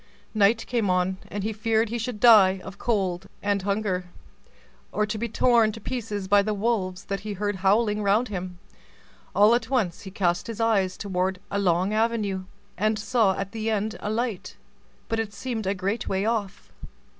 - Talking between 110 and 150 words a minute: No, average, 180 wpm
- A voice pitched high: Yes, high, 205 Hz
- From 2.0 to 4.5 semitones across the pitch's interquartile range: Yes, average, 2.7 semitones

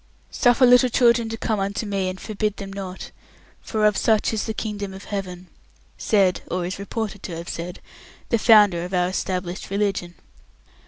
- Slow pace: No, average, 175 wpm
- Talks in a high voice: Yes, high, 200 Hz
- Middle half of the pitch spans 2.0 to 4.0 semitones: Yes, average, 2.9 semitones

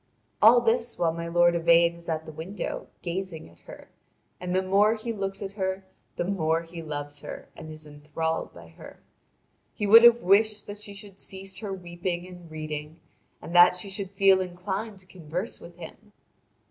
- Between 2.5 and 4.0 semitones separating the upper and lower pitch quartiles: Yes, average, 3.3 semitones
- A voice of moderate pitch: Yes, medium, 180 Hz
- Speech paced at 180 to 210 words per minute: Yes, average, 185 wpm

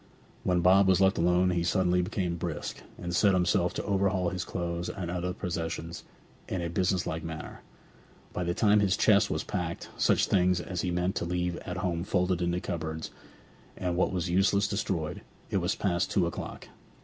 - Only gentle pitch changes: Yes, narrow, 1.5 semitones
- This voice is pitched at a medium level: No, very low, 90 Hz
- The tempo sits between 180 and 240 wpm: Yes, average, 190 wpm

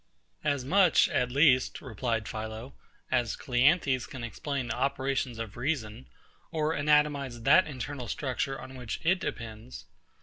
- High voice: No, low, 130 Hz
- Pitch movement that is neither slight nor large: Yes, average, 3.5 semitones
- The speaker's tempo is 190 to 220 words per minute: No, slow, 135 wpm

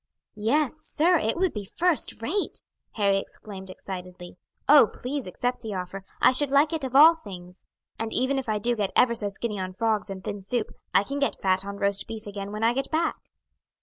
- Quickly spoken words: Yes, fast, 210 wpm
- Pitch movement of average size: No, wide, 6.0 semitones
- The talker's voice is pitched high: Yes, high, 220 Hz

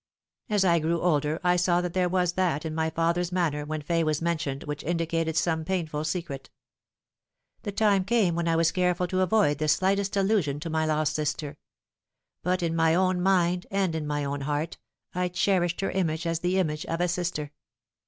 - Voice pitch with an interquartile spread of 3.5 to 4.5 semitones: No, narrow, 2.6 semitones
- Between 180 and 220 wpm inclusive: Yes, average, 195 wpm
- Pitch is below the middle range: No, medium, 170 Hz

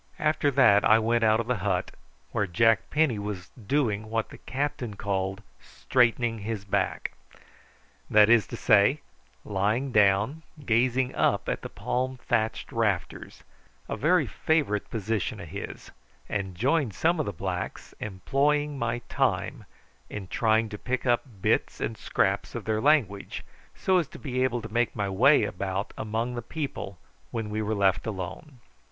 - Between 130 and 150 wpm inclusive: No, average, 160 wpm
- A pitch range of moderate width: Yes, average, 4.0 semitones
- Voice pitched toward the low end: Yes, low, 115 Hz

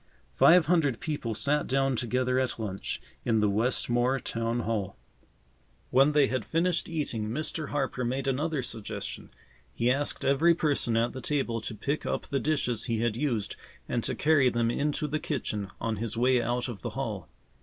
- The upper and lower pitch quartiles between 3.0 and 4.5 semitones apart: Yes, average, 4.0 semitones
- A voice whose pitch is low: Yes, low, 125 Hz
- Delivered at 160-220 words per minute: Yes, average, 175 wpm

